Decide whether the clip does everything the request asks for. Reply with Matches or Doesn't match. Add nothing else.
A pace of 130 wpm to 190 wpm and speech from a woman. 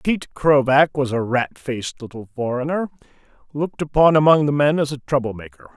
Doesn't match